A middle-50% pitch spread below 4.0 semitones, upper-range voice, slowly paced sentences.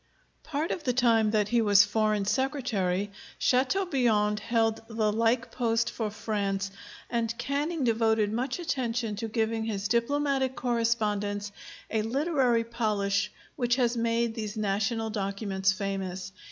Yes: average, 2.7 semitones; high, 225 Hz; slow, 130 wpm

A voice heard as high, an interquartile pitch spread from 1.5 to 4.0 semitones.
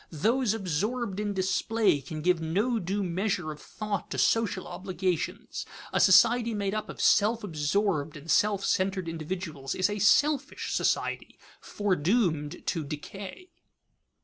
No: high, 195 Hz; average, 4.4 semitones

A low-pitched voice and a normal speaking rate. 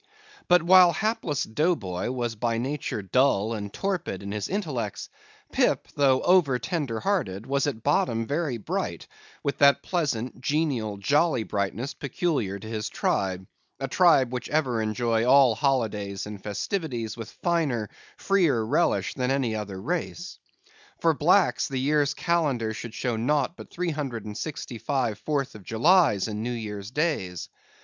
Yes: low, 130 Hz; average, 155 wpm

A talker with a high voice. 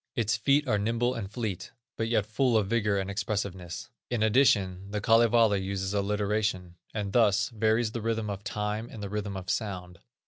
No: low, 105 Hz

